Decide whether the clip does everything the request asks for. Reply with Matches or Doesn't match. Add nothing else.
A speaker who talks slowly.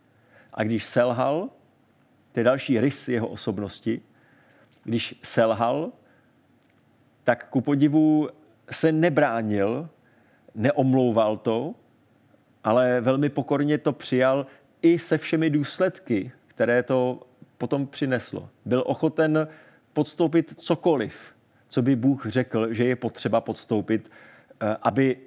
Matches